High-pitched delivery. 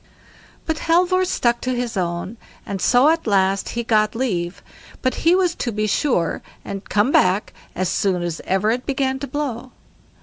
Yes: high, 235 Hz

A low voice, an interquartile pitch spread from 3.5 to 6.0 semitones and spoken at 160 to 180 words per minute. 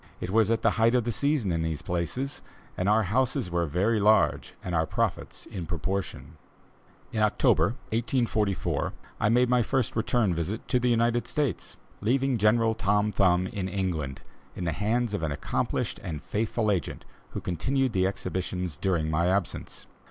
Yes: low, 105 Hz; average, 4.5 semitones; average, 170 wpm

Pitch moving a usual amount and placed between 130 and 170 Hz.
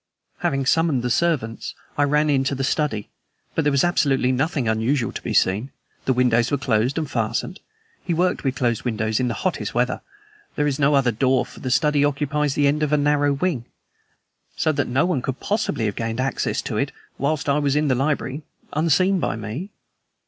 Yes: average, 3.3 semitones; medium, 140 Hz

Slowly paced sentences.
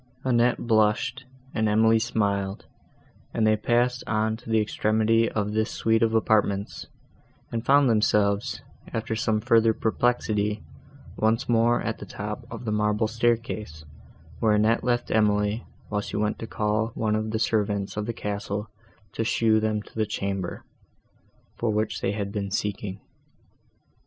No: average, 150 wpm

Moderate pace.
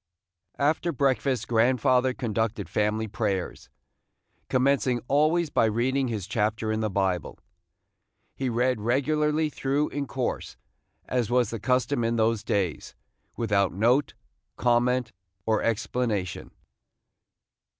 No: slow, 110 wpm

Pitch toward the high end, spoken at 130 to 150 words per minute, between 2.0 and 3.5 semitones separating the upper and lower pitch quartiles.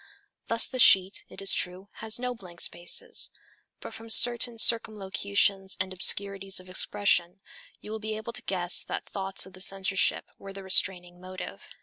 No: high, 195 Hz; average, 165 wpm; average, 2.8 semitones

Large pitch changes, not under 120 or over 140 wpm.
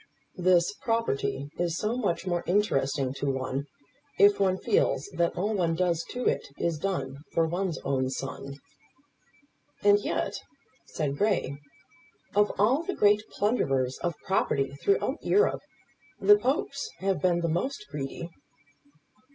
Yes: wide, 6.5 semitones; slow, 135 wpm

